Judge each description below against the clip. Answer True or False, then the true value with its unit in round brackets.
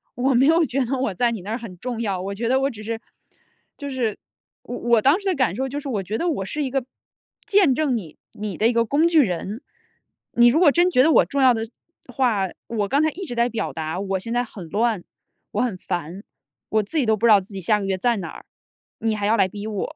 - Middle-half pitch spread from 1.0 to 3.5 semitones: False (4.8 semitones)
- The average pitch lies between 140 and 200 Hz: False (230 Hz)